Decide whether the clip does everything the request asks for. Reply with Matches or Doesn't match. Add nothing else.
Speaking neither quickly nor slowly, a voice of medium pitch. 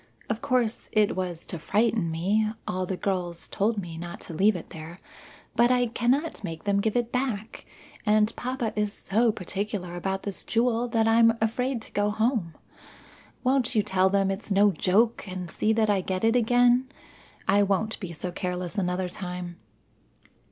Doesn't match